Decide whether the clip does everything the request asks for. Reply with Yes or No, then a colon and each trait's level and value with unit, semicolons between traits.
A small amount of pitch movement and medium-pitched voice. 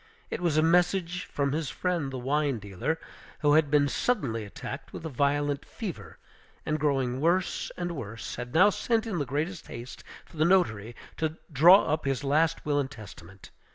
No: average, 4.2 semitones; medium, 150 Hz